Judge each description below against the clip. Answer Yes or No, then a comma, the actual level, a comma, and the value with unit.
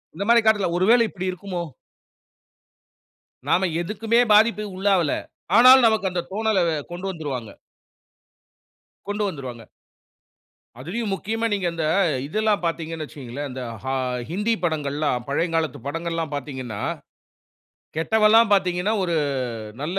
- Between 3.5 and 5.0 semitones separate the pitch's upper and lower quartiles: No, wide, 5.6 semitones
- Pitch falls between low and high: Yes, medium, 180 Hz